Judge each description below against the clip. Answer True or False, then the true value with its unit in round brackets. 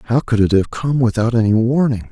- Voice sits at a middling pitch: False (115 Hz)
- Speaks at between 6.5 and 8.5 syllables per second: False (5.8 syllables/s)